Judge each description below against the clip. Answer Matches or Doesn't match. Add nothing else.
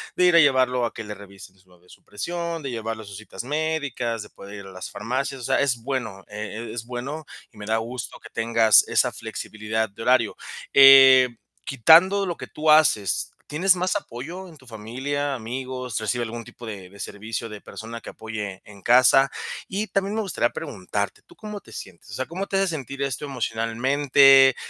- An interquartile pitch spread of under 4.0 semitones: Doesn't match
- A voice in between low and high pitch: Doesn't match